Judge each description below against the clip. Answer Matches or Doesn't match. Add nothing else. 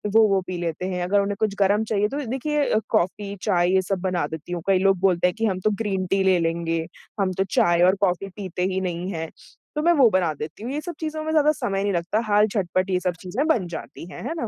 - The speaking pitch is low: Doesn't match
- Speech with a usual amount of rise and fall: Matches